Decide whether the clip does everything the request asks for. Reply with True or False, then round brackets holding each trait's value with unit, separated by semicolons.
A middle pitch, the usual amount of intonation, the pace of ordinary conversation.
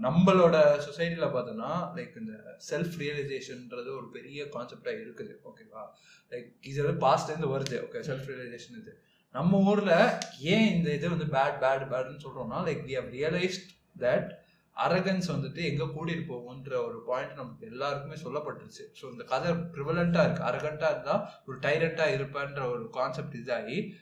True (155 Hz; 4.5 semitones; 120 wpm)